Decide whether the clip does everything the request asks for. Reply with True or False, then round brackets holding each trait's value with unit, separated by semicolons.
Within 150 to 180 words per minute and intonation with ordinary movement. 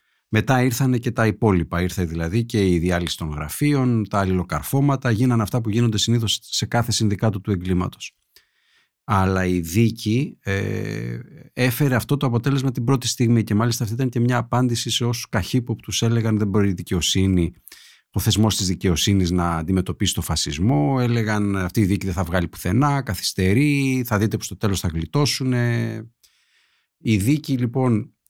True (165 wpm; 4.4 semitones)